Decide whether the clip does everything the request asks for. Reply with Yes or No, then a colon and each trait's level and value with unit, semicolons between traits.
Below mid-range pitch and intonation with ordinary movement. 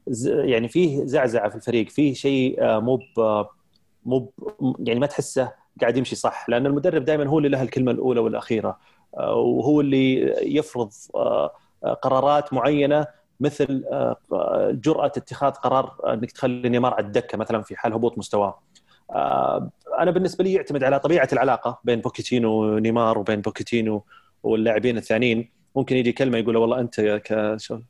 Yes: low, 130 Hz; average, 3.6 semitones